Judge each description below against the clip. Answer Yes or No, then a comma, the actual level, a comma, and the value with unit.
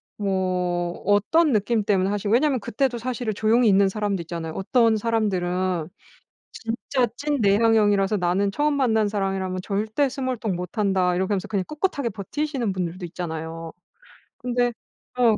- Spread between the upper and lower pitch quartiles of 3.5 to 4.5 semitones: Yes, average, 4.2 semitones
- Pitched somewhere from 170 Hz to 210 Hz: Yes, high, 205 Hz